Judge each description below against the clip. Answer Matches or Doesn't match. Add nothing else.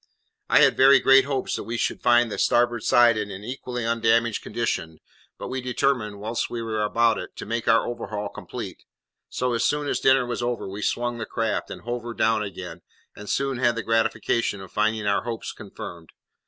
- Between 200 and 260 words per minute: Matches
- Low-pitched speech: Matches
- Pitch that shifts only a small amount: Matches